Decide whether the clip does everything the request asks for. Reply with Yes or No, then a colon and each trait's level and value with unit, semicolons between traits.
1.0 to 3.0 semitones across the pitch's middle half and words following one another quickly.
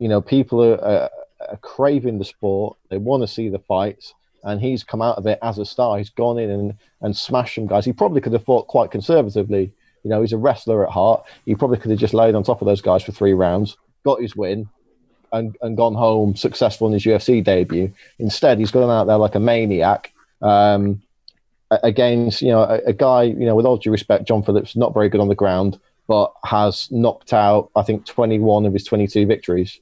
Yes: narrow, 2.4 semitones; fast, 225 wpm